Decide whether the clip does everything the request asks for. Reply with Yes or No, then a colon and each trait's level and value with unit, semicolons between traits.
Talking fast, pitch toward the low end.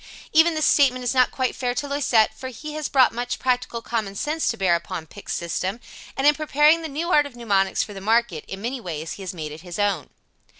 No: fast, 240 wpm; high, 240 Hz